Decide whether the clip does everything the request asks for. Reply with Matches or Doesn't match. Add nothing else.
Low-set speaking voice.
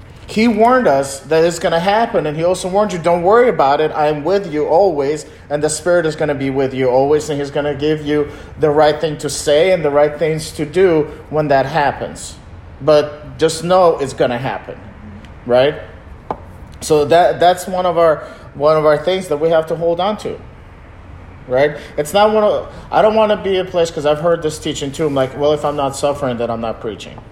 Doesn't match